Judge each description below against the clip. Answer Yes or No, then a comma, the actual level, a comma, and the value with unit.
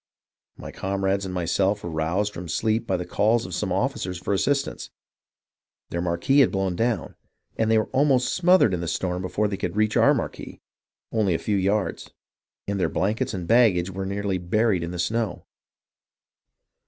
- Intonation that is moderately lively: Yes, average, 3.5 semitones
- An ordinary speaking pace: Yes, average, 180 wpm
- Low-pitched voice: Yes, low, 100 Hz